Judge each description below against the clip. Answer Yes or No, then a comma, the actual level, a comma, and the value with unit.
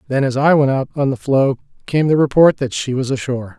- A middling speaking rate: No, fast, 250 wpm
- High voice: No, low, 135 Hz